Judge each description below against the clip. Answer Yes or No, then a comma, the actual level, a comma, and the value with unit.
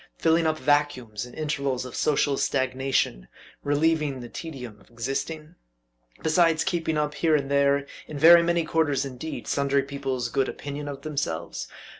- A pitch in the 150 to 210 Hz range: No, medium, 140 Hz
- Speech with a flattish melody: No, average, 3.0 semitones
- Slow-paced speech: No, average, 150 wpm